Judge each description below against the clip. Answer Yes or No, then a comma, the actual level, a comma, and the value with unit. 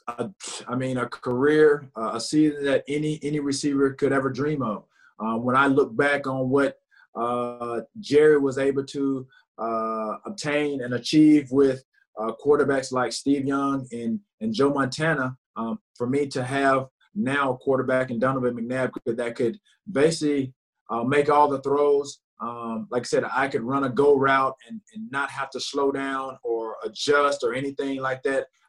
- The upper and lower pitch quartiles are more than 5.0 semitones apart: No, narrow, 2.5 semitones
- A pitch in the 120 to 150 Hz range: Yes, low, 135 Hz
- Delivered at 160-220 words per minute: Yes, average, 175 wpm